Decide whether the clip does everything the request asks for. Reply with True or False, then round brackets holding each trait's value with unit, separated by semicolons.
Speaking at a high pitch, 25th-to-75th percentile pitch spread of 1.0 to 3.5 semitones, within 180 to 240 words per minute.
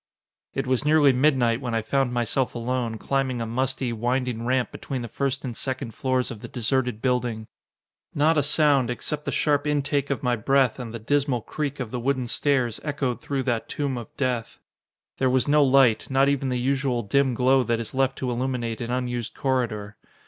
False (130 Hz; 2.4 semitones; 195 wpm)